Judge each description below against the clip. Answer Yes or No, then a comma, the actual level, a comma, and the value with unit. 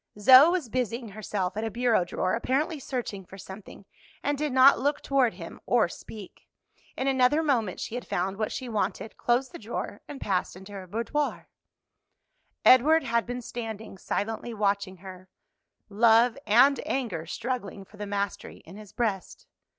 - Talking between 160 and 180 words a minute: Yes, average, 165 wpm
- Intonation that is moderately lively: Yes, average, 4.3 semitones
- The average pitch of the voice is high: Yes, high, 225 Hz